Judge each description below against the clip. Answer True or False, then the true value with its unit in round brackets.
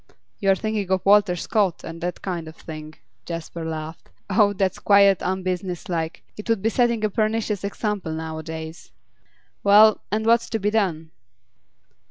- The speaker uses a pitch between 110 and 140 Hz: False (190 Hz)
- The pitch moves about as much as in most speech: True (4.3 semitones)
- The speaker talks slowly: False (155 wpm)